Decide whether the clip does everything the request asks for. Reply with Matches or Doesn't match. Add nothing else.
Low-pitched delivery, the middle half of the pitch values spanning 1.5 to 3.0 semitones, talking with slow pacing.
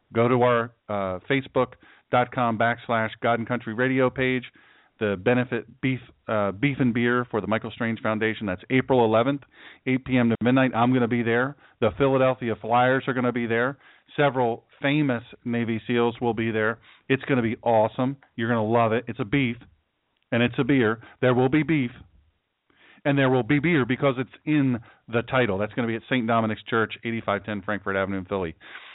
Doesn't match